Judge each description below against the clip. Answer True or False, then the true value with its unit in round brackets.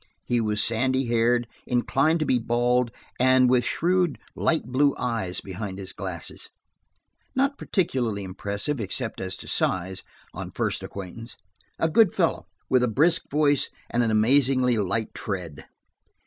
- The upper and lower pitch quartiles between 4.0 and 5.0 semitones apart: True (4.6 semitones)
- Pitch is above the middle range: False (120 Hz)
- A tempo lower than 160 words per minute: True (145 wpm)